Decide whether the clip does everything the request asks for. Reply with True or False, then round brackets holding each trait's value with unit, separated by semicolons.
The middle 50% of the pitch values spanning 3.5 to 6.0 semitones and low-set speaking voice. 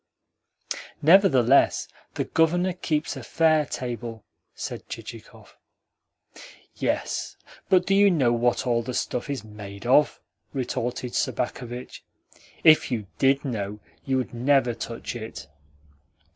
True (4.4 semitones; 125 Hz)